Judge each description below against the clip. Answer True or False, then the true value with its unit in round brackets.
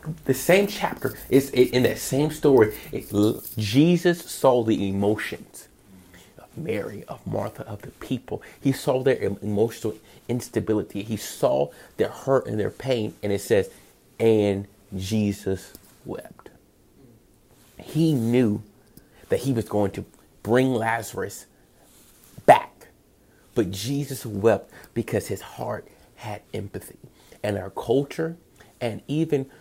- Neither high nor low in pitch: False (115 Hz)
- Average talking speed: False (125 wpm)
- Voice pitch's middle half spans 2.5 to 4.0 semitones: False (4.6 semitones)